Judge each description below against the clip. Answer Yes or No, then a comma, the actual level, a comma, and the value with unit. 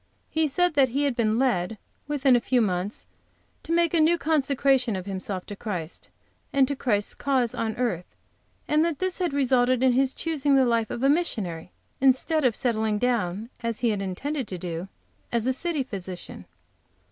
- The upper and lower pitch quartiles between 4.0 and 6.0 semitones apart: Yes, average, 5.2 semitones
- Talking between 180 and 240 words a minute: Yes, average, 185 wpm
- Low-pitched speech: No, very high, 250 Hz